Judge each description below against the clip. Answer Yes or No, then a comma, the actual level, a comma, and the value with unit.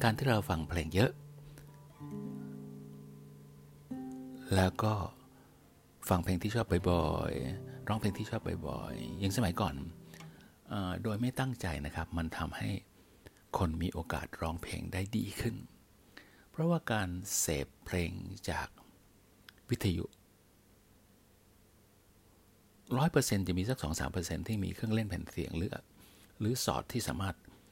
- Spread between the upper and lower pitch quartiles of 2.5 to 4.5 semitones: No, average, 5.1 semitones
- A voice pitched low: Yes, low, 100 Hz